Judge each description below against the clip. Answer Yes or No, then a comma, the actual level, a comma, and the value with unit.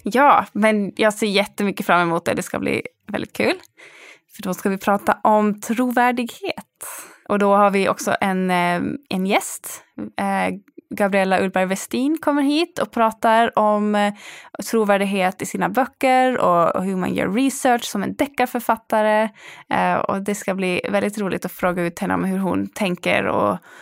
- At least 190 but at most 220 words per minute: No, average, 160 wpm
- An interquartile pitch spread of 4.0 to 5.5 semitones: Yes, average, 4.3 semitones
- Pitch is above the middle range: Yes, high, 210 Hz